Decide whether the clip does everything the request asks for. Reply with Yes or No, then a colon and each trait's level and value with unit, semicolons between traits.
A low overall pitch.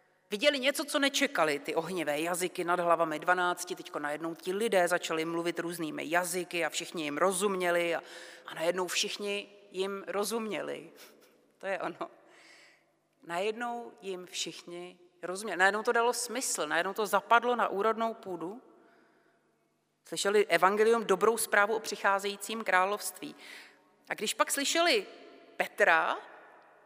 No: high, 190 Hz